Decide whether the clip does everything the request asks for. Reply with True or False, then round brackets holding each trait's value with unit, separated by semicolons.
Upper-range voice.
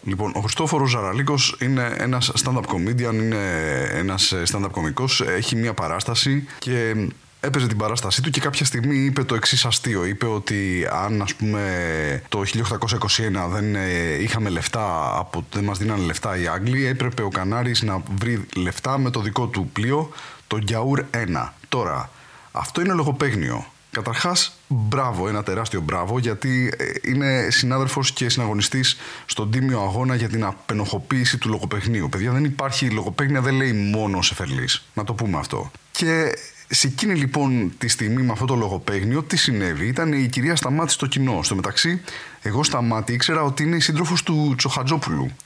False (120 Hz)